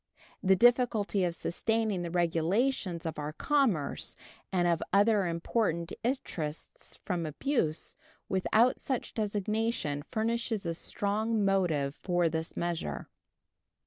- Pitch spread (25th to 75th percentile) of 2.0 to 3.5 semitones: No, average, 5.0 semitones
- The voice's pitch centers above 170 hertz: Yes, high, 190 Hz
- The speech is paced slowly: Yes, slow, 115 wpm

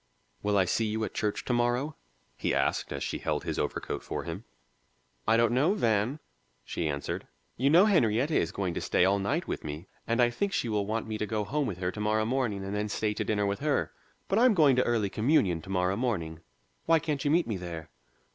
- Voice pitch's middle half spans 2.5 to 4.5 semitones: No, average, 5.2 semitones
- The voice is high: No, low, 110 Hz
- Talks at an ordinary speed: No, fast, 230 wpm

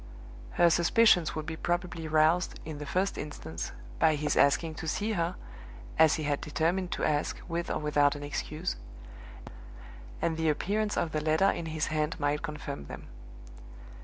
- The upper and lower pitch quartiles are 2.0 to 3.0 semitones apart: Yes, narrow, 2.4 semitones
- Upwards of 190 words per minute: No, average, 165 wpm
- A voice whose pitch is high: No, medium, 160 Hz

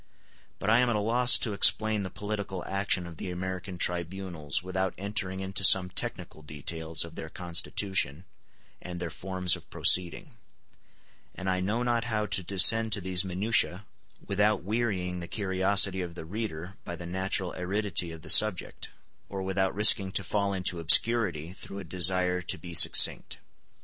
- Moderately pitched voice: No, very low, 95 Hz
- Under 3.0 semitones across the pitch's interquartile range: Yes, narrow, 2.4 semitones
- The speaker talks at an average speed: Yes, average, 165 wpm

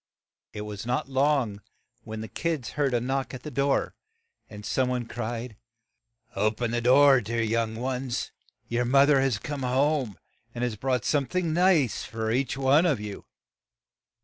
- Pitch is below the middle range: Yes, low, 125 Hz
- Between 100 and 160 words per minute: No, average, 175 wpm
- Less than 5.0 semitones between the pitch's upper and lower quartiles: Yes, average, 3.3 semitones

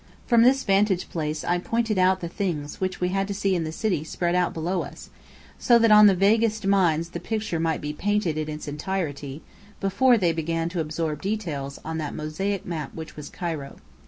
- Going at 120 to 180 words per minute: No, average, 200 wpm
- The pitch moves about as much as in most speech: Yes, average, 4.2 semitones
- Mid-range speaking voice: Yes, medium, 180 Hz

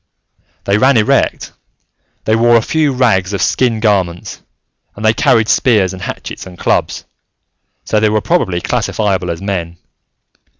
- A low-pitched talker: Yes, low, 105 Hz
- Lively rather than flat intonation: No, average, 3.6 semitones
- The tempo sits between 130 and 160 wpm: Yes, average, 145 wpm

